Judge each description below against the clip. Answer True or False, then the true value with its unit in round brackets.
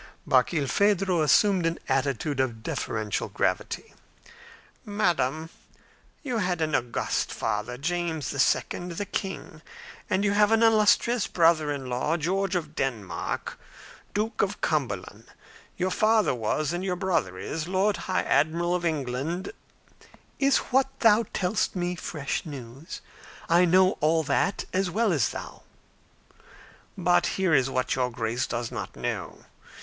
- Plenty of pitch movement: True (6.0 semitones)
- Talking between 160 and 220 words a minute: False (135 wpm)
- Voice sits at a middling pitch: True (170 Hz)